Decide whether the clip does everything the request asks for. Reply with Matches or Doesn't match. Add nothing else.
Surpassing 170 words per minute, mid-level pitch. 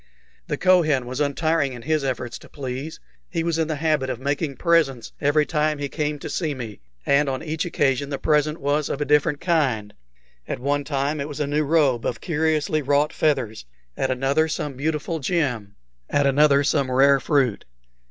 Matches